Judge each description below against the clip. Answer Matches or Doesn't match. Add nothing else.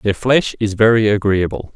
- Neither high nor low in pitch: Doesn't match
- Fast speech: Doesn't match